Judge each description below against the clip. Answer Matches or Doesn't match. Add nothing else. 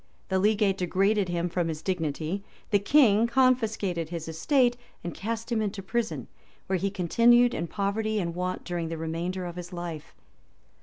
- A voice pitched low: Doesn't match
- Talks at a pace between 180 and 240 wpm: Doesn't match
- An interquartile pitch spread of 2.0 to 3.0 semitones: Doesn't match